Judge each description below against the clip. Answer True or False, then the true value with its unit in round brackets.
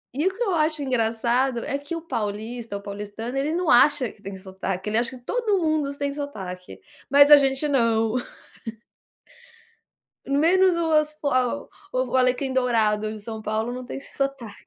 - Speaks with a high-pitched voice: True (255 Hz)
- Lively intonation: False (4.9 semitones)